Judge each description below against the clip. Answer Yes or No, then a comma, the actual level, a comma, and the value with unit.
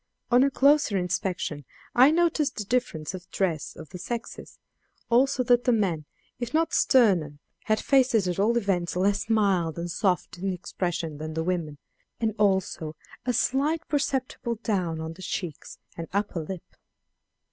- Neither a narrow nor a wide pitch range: No, wide, 6.0 semitones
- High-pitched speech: Yes, high, 195 Hz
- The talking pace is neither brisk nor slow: Yes, average, 160 wpm